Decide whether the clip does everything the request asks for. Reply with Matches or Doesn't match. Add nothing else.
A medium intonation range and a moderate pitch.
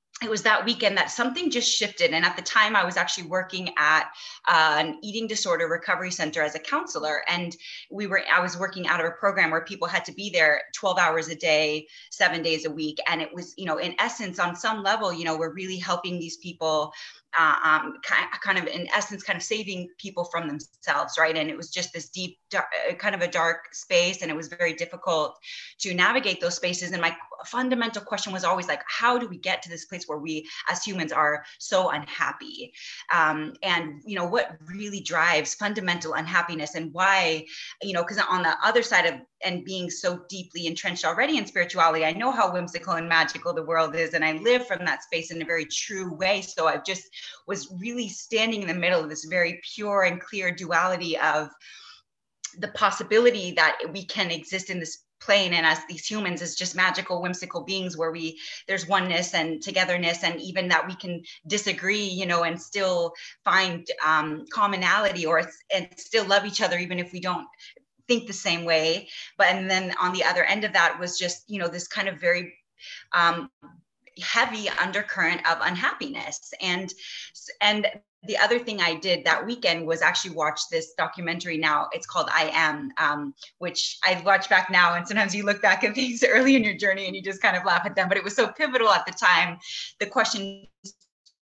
Matches